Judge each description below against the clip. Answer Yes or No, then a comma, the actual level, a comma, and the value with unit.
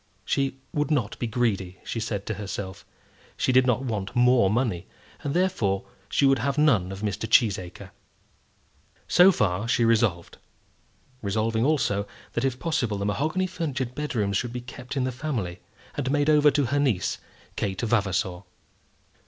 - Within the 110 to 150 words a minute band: No, average, 160 wpm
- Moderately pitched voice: No, low, 120 Hz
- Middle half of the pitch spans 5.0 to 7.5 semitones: Yes, wide, 5.4 semitones